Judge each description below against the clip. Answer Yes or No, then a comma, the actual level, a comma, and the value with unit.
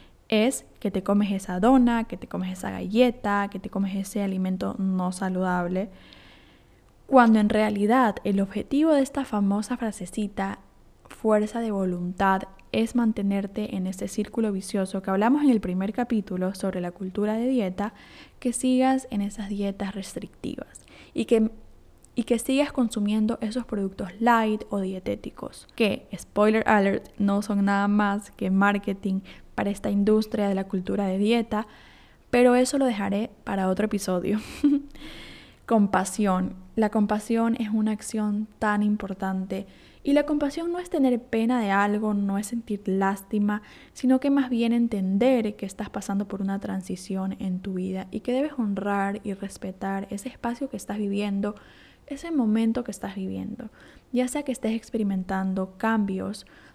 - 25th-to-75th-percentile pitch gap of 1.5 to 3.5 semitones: Yes, average, 3.1 semitones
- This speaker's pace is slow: No, average, 155 wpm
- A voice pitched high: Yes, high, 210 Hz